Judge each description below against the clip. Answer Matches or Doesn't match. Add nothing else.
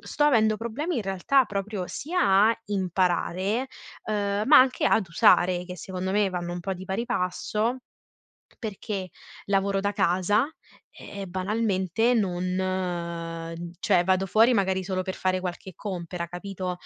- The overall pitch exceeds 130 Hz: Matches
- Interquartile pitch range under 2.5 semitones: Doesn't match